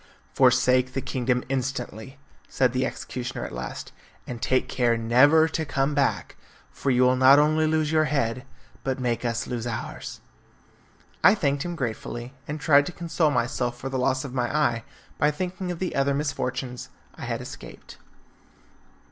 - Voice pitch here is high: No, low, 130 Hz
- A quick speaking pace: No, average, 165 wpm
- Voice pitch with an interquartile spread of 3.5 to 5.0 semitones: No, average, 3.1 semitones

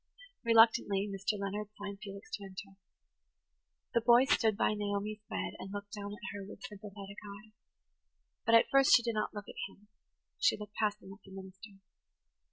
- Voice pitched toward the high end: Yes, high, 205 Hz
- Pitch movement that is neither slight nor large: No, narrow, 1.6 semitones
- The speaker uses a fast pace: No, average, 175 wpm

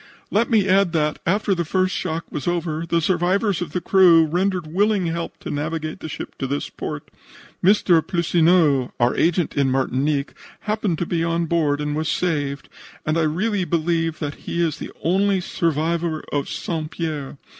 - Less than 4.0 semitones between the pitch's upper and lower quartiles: Yes, average, 2.9 semitones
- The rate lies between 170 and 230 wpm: Yes, average, 175 wpm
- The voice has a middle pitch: Yes, medium, 165 Hz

